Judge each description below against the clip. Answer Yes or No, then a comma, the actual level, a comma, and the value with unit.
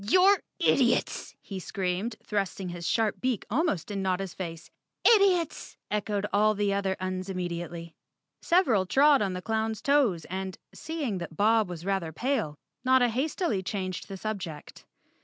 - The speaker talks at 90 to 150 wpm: Yes, average, 145 wpm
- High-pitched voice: Yes, high, 200 Hz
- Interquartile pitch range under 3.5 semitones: No, average, 4.6 semitones